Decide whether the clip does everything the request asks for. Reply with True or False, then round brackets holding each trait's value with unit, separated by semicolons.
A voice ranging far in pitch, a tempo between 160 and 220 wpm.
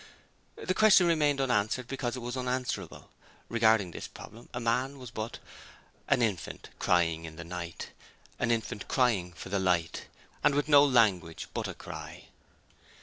False (6.2 semitones; 150 wpm)